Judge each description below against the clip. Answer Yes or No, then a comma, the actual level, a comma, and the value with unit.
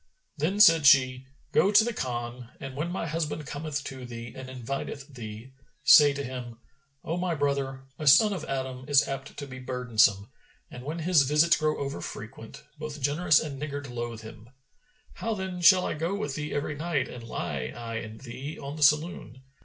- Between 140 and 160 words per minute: No, average, 190 wpm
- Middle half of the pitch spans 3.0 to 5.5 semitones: Yes, average, 3.5 semitones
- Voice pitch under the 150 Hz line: Yes, medium, 140 Hz